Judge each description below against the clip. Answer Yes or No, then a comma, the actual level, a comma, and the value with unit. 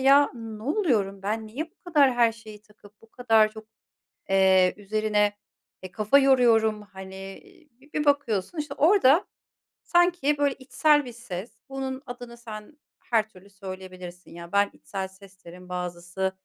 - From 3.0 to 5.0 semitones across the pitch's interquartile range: No, wide, 5.5 semitones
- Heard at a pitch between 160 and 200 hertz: No, high, 215 Hz